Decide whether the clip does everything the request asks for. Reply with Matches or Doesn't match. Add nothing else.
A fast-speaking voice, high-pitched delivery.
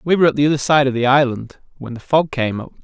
Doesn't match